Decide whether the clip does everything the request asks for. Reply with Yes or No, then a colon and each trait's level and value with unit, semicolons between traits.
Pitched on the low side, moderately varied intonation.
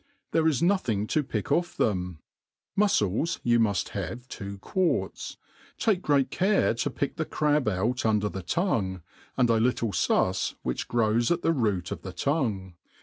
No: low, 120 Hz; wide, 7.4 semitones